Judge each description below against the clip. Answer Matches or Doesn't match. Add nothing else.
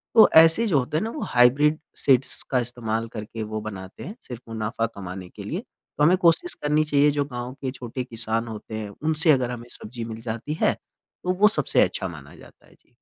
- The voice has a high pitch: Doesn't match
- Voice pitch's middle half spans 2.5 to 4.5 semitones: Doesn't match